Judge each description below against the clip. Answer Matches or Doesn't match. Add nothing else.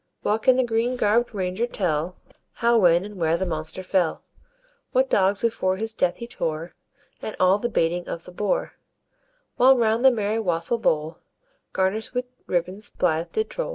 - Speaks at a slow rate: Doesn't match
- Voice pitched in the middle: Doesn't match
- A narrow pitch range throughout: Doesn't match